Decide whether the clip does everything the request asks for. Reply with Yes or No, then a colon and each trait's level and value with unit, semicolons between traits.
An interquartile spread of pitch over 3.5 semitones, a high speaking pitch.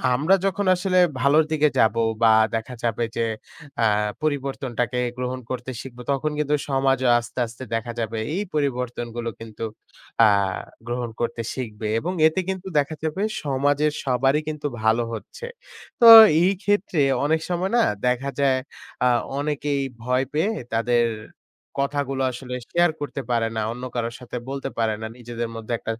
No: average, 4.1 semitones; low, 130 Hz